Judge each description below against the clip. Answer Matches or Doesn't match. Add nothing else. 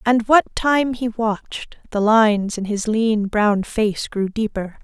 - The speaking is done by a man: Doesn't match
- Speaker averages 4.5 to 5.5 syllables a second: Doesn't match